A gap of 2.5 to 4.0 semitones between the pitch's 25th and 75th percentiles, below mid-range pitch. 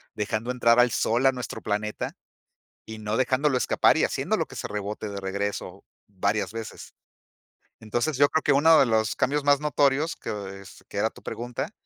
No: average, 4.5 semitones; low, 115 Hz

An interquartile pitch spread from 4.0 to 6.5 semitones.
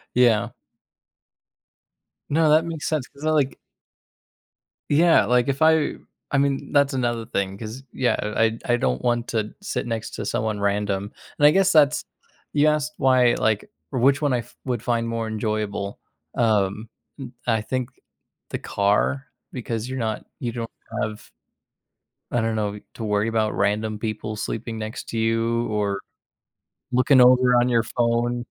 No: average, 3.4 semitones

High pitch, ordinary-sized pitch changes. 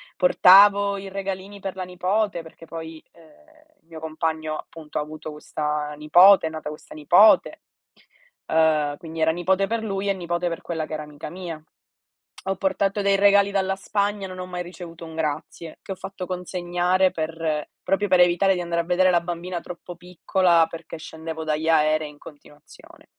No: medium, 175 Hz; average, 3.2 semitones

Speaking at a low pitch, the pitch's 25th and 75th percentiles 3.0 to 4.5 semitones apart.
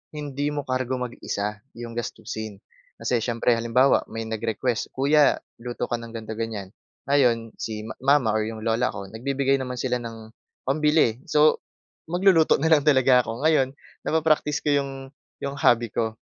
Yes: low, 125 Hz; average, 3.7 semitones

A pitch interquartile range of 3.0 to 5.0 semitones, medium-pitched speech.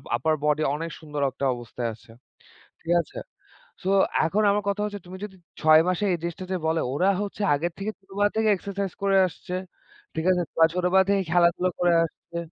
Yes: average, 3.5 semitones; medium, 180 Hz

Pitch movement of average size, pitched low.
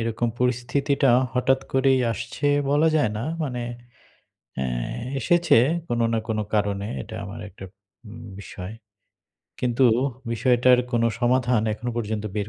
Yes: average, 3.2 semitones; low, 120 Hz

